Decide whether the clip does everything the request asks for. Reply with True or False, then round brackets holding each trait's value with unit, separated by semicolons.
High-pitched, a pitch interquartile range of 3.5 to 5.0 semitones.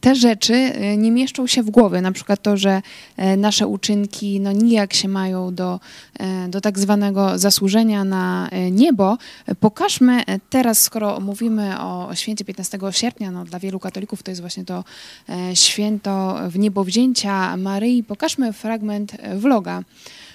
False (205 Hz; 2.9 semitones)